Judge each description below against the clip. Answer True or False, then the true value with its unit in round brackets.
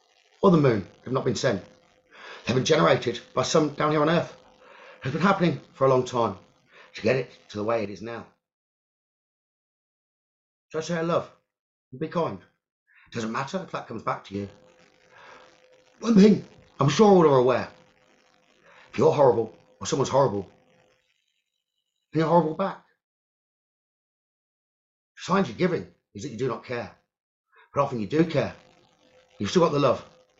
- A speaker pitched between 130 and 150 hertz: True (140 Hz)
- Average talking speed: True (165 wpm)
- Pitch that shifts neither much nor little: False (6.5 semitones)